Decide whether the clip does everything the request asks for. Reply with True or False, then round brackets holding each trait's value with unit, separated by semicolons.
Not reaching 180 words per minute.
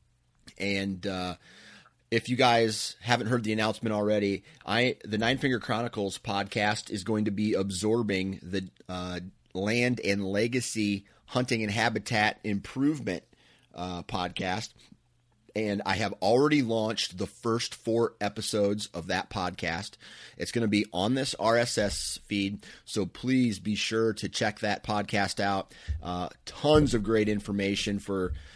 True (140 wpm)